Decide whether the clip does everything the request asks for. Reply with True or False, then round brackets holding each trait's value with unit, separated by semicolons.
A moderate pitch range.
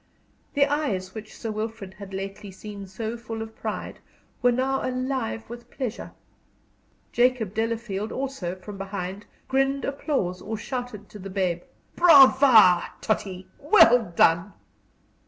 True (4.7 semitones)